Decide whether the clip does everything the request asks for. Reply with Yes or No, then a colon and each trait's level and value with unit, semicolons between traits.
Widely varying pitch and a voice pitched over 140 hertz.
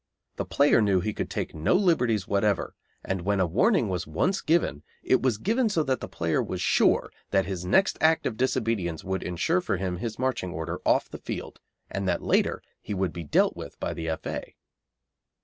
No: wide, 6.6 semitones; low, 100 Hz